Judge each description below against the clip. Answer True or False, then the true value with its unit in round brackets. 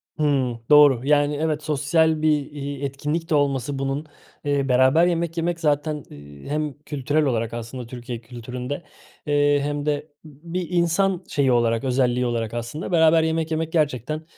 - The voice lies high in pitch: False (145 Hz)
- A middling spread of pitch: True (3.6 semitones)